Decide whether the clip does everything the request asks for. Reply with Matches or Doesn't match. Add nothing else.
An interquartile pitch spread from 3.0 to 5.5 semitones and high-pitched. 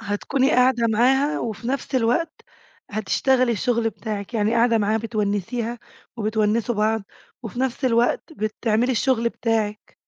Doesn't match